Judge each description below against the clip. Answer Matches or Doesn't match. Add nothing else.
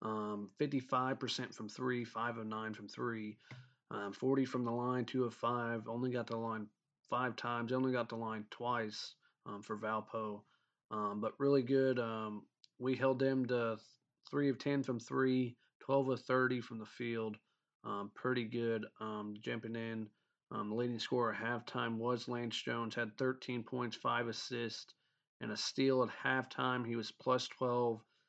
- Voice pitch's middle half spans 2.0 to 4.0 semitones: Matches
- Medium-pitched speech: Doesn't match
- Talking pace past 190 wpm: Doesn't match